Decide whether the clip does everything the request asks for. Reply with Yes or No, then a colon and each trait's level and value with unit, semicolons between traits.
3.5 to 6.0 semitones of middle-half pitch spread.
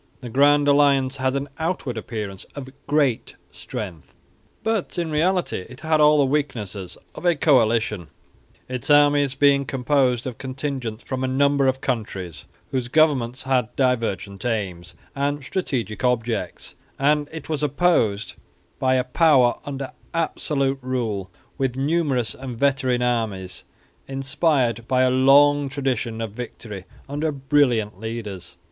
Yes: average, 4.0 semitones